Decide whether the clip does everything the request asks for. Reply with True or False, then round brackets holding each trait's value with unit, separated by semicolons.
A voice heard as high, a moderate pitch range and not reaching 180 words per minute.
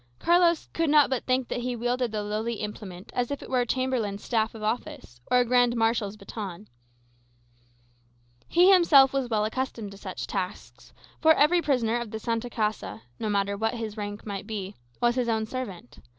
False (230 Hz; 3.4 semitones; 190 wpm)